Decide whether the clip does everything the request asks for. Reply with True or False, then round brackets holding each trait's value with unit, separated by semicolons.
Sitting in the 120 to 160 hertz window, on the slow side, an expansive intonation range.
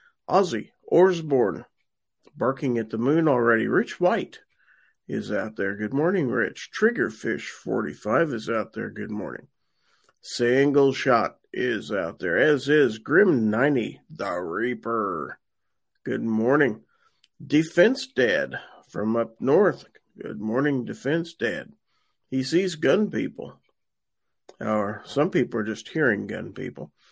True (135 Hz; 120 wpm; 5.7 semitones)